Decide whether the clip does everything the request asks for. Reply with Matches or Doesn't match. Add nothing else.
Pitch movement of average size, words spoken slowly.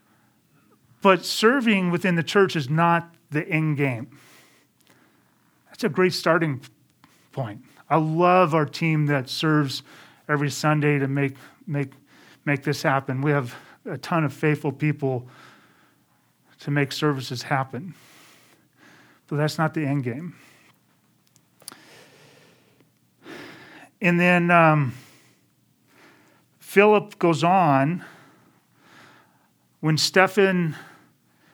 Matches